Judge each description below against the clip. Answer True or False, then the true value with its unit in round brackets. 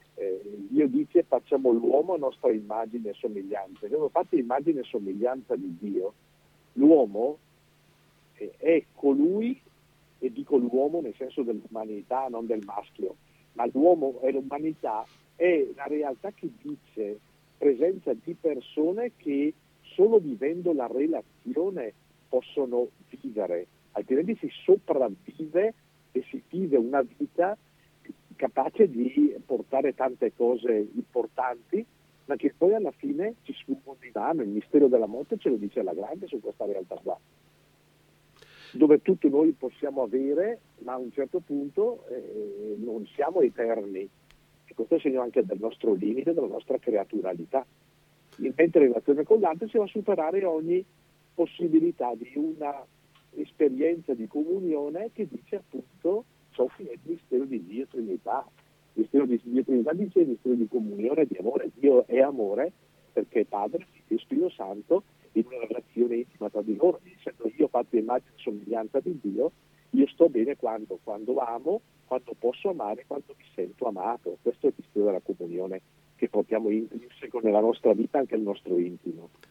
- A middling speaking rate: True (150 wpm)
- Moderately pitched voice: True (160 Hz)